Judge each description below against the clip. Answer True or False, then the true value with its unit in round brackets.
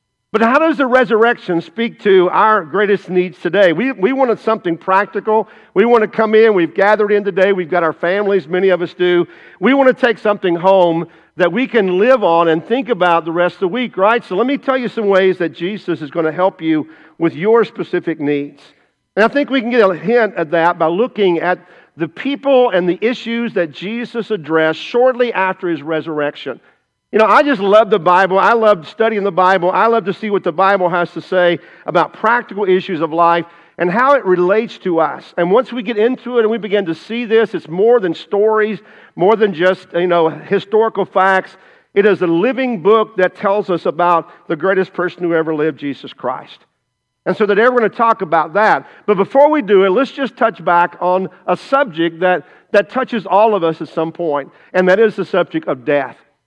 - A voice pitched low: False (190 Hz)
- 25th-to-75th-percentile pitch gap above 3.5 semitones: True (4.5 semitones)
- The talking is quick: True (220 wpm)